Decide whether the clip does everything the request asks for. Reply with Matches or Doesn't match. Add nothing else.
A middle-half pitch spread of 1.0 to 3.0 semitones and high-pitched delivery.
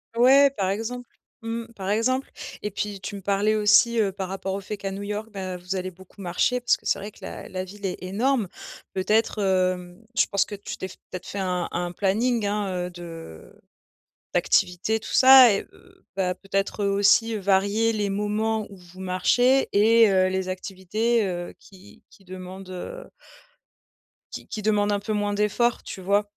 Matches